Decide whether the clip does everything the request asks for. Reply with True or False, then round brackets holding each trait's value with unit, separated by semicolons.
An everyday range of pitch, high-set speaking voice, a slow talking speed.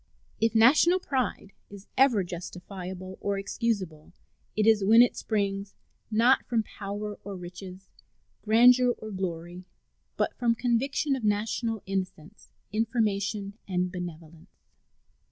True (3.5 semitones; 205 Hz; 120 wpm)